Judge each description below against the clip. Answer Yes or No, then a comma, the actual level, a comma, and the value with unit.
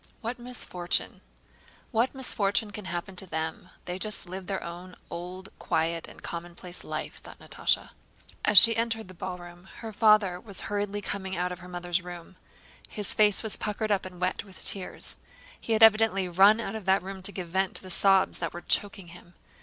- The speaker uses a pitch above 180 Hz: Yes, high, 190 Hz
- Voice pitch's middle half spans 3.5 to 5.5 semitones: No, average, 2.8 semitones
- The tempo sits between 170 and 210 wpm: Yes, average, 190 wpm